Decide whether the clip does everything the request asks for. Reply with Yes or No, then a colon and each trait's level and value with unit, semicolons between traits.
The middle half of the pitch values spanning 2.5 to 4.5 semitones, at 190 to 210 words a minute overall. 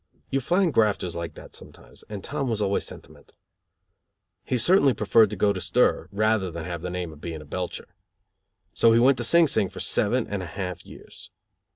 No: wide, 5.5 semitones; average, 200 wpm